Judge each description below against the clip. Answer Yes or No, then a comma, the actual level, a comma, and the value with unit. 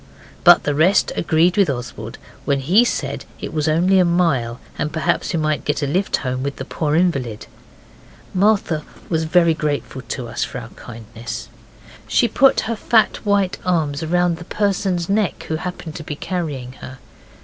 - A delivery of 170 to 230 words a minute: Yes, average, 175 wpm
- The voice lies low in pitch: No, medium, 160 Hz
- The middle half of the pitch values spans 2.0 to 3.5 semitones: No, average, 4.5 semitones